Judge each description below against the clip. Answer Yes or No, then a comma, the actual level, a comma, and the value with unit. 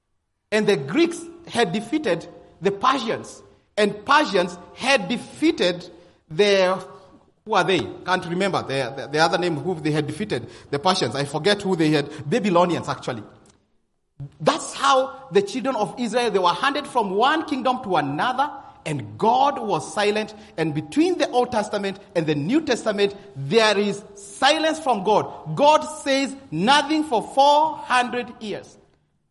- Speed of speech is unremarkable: Yes, average, 150 wpm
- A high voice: Yes, high, 205 Hz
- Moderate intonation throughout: No, wide, 7.0 semitones